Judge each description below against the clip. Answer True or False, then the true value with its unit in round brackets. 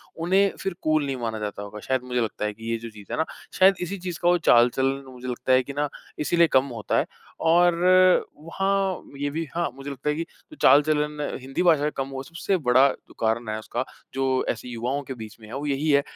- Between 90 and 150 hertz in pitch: True (140 Hz)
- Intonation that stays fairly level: False (4.9 semitones)